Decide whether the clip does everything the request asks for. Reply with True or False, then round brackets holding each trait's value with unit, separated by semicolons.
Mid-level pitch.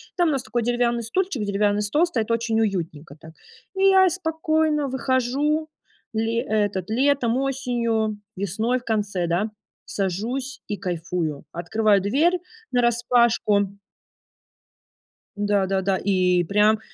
False (225 Hz)